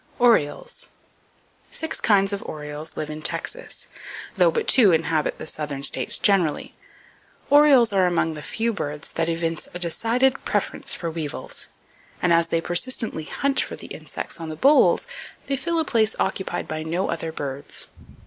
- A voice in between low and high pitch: Yes, medium, 175 Hz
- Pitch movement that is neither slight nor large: No, wide, 7.0 semitones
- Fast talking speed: No, average, 160 wpm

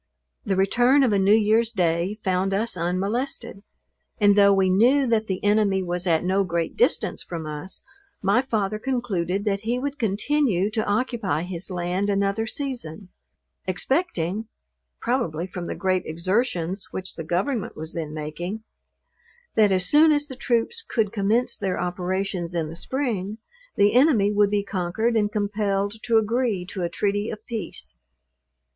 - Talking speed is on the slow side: No, average, 160 wpm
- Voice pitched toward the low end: No, high, 200 Hz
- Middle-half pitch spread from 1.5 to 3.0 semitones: No, average, 3.8 semitones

